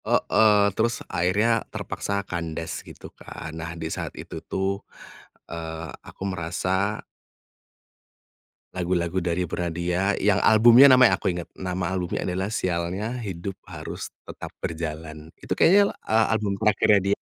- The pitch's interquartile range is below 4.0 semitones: Yes, average, 3.4 semitones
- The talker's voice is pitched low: Yes, very low, 95 Hz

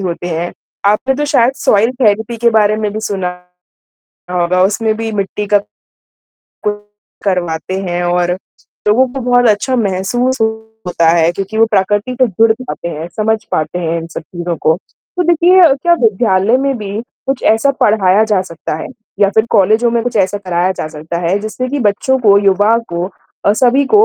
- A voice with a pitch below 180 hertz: No, high, 205 Hz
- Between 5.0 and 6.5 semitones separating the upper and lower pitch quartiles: No, average, 4.1 semitones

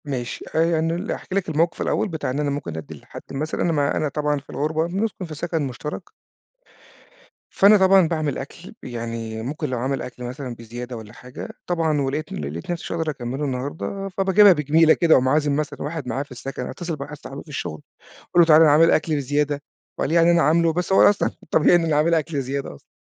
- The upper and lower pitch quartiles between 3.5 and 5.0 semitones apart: Yes, average, 3.8 semitones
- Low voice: No, medium, 150 Hz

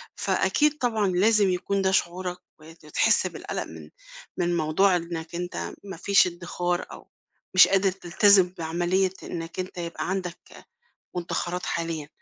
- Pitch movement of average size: No, narrow, 2.0 semitones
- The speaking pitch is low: No, medium, 180 Hz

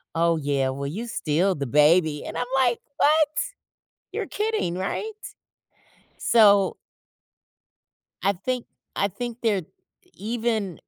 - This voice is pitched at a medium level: No, high, 195 Hz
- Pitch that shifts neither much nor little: No, wide, 7.0 semitones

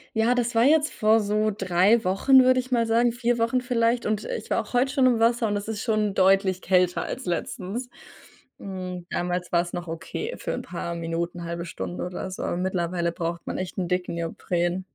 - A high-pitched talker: Yes, high, 195 Hz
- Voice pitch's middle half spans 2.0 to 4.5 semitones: No, average, 5.0 semitones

